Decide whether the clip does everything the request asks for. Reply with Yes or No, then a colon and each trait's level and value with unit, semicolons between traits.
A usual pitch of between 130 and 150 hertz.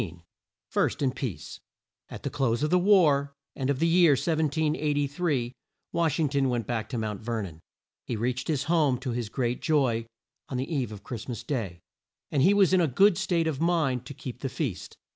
Yes: medium, 140 Hz